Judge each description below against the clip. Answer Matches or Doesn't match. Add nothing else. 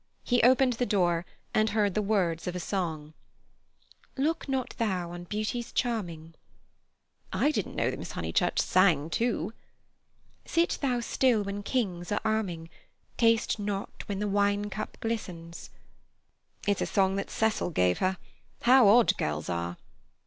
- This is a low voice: Doesn't match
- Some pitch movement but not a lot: Matches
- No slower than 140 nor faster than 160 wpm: Matches